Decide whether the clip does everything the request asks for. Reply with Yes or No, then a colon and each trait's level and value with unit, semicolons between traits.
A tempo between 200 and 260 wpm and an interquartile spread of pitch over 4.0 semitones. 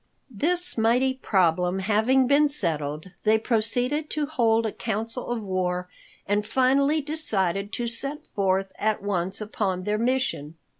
No: average, 140 wpm; average, 5.3 semitones